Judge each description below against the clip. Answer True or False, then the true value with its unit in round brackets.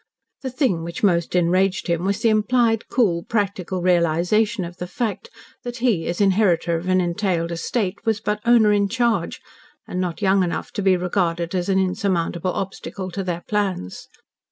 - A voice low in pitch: False (190 Hz)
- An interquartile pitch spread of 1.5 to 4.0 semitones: True (3.4 semitones)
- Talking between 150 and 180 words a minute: True (175 wpm)